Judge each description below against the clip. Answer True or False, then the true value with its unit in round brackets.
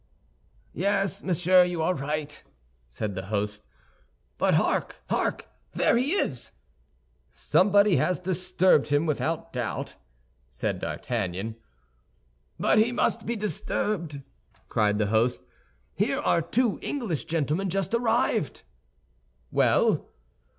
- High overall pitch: False (170 Hz)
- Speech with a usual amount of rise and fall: False (8.0 semitones)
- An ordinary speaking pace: False (110 wpm)